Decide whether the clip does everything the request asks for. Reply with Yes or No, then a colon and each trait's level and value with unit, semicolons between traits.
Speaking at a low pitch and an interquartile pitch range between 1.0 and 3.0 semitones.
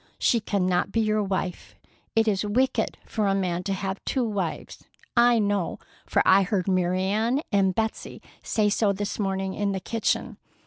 No: high, 200 Hz; narrow, 2.4 semitones